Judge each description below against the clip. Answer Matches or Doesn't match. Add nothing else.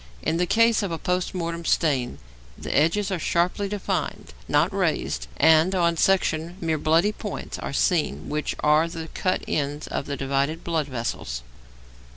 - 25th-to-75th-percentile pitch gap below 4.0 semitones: Matches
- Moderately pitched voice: Matches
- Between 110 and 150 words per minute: Doesn't match